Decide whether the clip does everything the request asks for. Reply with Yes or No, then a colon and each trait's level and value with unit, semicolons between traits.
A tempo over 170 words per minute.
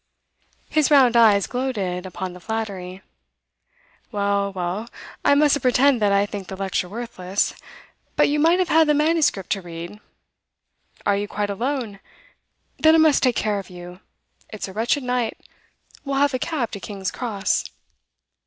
No: average, 160 wpm